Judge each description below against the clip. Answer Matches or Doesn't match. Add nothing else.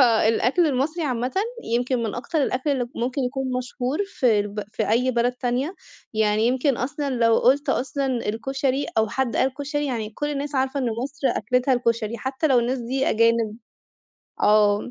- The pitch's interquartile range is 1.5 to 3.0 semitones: Matches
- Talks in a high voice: Matches